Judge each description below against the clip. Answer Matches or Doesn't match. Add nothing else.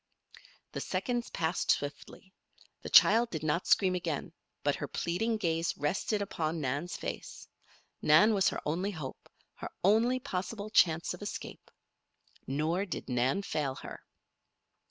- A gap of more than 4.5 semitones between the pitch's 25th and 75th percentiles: Matches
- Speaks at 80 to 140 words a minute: Matches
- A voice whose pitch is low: Doesn't match